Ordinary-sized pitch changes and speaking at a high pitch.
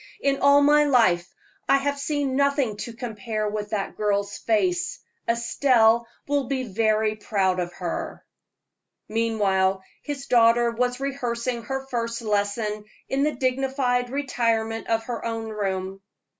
Yes: average, 4.0 semitones; high, 230 Hz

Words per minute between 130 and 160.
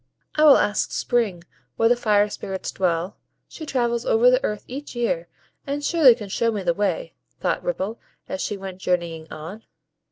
No: average, 180 wpm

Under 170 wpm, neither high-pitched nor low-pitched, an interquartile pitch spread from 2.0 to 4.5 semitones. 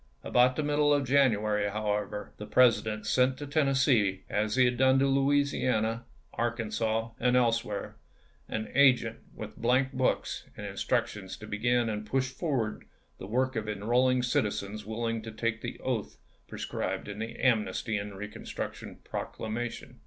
No: average, 155 wpm; low, 115 Hz; average, 3.3 semitones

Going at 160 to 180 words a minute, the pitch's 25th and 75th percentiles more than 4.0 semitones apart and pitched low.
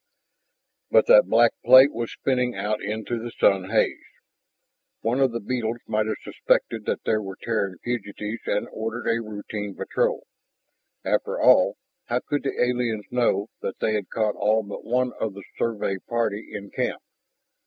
No: average, 165 wpm; average, 2.8 semitones; low, 110 Hz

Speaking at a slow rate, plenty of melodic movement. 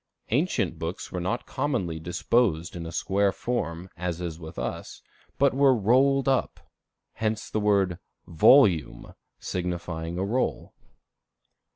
Yes: slow, 120 wpm; wide, 6.5 semitones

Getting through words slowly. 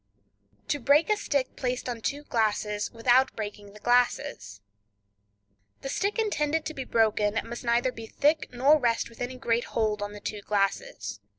No: average, 165 wpm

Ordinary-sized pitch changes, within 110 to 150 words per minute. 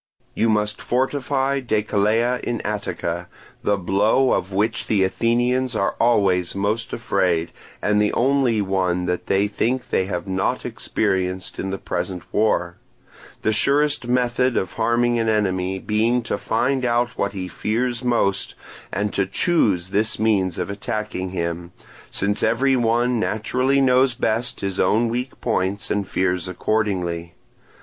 Yes: average, 4.1 semitones; average, 145 wpm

